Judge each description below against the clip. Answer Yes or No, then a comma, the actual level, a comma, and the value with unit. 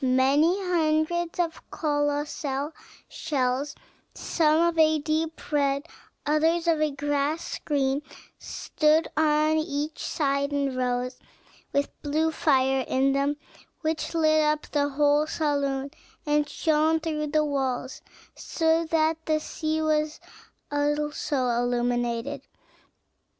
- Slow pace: Yes, slow, 115 wpm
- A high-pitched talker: Yes, very high, 295 Hz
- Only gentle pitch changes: Yes, narrow, 2.1 semitones